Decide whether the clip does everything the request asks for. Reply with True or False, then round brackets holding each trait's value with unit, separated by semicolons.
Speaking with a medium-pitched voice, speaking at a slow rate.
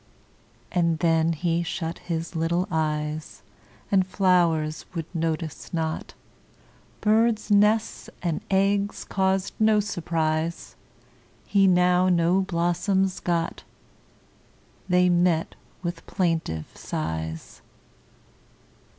True (175 Hz; 90 wpm)